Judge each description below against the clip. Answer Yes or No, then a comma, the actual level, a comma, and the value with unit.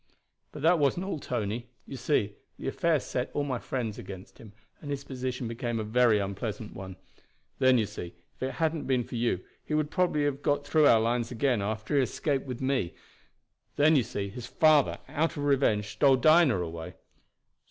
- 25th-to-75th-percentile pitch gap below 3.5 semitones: No, average, 4.8 semitones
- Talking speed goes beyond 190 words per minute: Yes, average, 200 wpm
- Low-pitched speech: Yes, low, 130 Hz